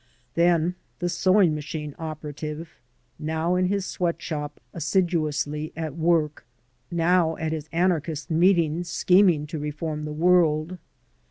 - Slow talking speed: Yes, slow, 120 wpm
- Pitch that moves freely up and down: No, narrow, 2.5 semitones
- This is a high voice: No, medium, 160 Hz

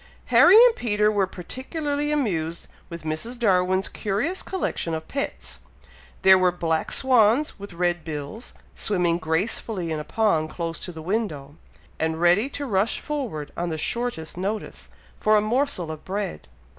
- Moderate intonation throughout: No, wide, 6.1 semitones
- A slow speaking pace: No, average, 155 wpm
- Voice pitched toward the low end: No, high, 190 Hz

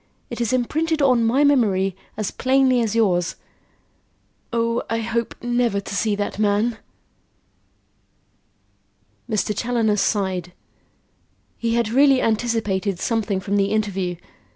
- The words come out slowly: Yes, slow, 120 wpm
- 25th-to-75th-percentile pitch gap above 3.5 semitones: No, average, 3.1 semitones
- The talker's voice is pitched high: Yes, high, 225 Hz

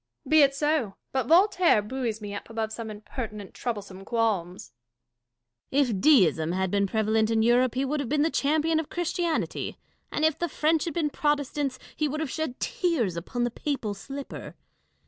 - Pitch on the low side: No, very high, 255 Hz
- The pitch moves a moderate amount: No, wide, 6.0 semitones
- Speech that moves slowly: No, average, 185 wpm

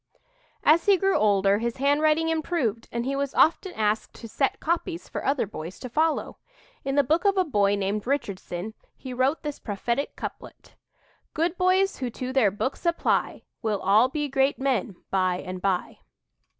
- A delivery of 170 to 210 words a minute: Yes, average, 175 wpm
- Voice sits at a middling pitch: No, very high, 265 Hz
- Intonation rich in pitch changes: Yes, wide, 7.0 semitones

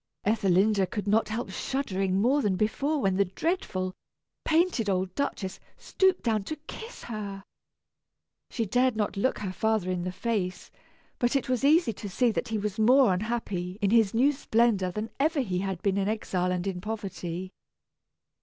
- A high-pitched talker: Yes, high, 210 Hz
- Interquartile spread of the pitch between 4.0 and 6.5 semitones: Yes, average, 4.3 semitones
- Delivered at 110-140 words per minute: No, average, 175 wpm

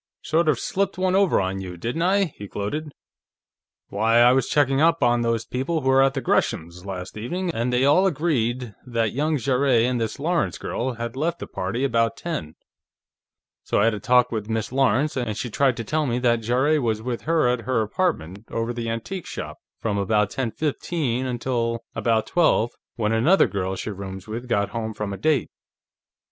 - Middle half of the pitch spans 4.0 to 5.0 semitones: Yes, average, 4.5 semitones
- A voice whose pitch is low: Yes, low, 120 Hz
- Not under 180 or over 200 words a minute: Yes, average, 195 wpm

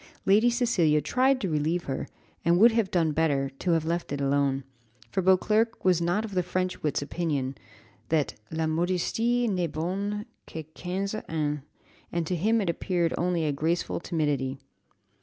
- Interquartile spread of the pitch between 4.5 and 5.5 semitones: No, average, 3.9 semitones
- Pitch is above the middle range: No, medium, 170 Hz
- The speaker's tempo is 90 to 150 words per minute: No, average, 165 wpm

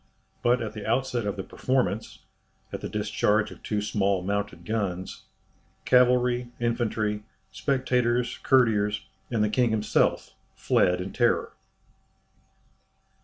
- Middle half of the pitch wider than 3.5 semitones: No, average, 3.0 semitones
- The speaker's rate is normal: No, slow, 120 wpm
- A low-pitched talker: Yes, low, 110 Hz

